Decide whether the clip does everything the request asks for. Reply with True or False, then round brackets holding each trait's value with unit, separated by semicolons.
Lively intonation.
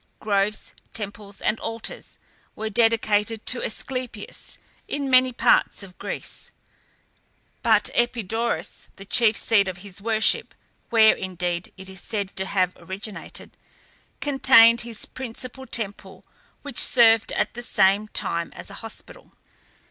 False (3.0 semitones)